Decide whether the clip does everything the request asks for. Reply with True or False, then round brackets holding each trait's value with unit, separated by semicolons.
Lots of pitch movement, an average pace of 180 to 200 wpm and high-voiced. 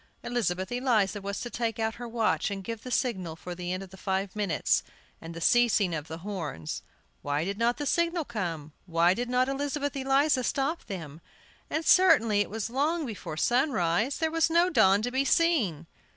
True (6.7 semitones; 195 wpm; 225 Hz)